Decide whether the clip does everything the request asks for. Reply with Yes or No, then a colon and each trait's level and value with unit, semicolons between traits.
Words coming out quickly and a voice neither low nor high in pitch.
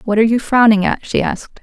No: fast, 260 wpm; high, 225 Hz